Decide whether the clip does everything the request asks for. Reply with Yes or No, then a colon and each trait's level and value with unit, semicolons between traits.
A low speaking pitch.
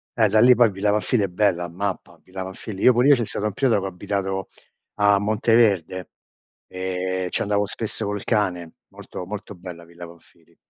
Yes: low, 100 Hz